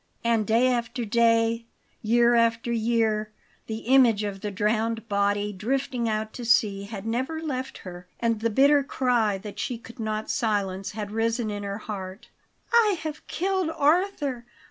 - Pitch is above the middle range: Yes, high, 230 Hz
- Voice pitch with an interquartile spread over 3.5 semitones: No, average, 3.0 semitones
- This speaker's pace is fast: No, average, 160 wpm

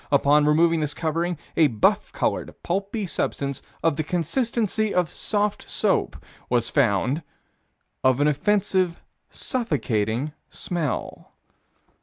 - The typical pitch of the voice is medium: Yes, medium, 160 Hz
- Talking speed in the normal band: No, slow, 110 wpm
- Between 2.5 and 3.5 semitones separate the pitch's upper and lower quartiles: No, average, 5.0 semitones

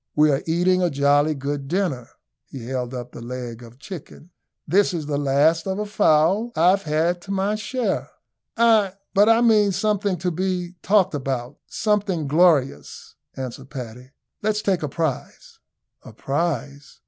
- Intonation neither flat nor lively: No, wide, 6.2 semitones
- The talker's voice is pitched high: No, medium, 165 Hz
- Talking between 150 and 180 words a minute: Yes, average, 160 wpm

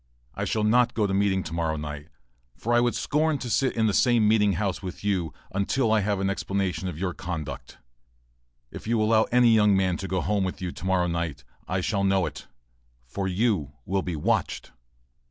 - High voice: No, low, 100 Hz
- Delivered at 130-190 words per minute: No, fast, 205 wpm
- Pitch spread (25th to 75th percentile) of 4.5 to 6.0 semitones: No, average, 3.4 semitones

